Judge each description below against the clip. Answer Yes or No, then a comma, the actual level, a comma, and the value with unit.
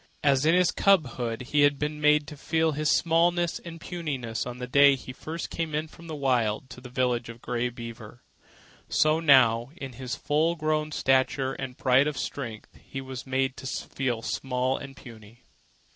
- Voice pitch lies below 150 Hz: Yes, low, 135 Hz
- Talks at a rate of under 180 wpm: No, average, 185 wpm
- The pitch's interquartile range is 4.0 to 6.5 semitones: No, average, 3.6 semitones